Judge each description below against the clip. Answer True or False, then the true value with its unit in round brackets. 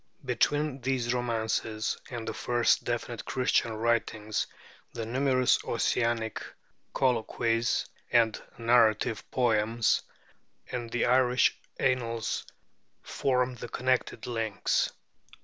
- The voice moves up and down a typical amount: False (1.9 semitones)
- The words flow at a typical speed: False (95 wpm)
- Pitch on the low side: True (120 Hz)